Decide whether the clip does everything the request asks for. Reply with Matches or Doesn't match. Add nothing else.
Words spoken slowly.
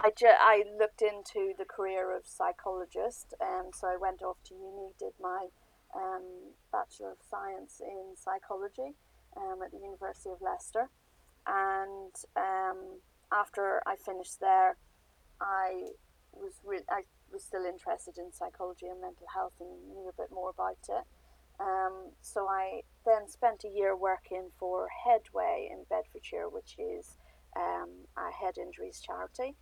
Doesn't match